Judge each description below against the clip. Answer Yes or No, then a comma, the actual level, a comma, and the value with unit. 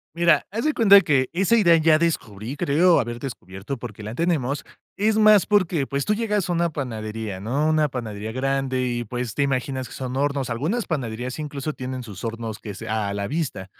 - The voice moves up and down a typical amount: No, wide, 6.3 semitones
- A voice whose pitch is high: No, low, 135 Hz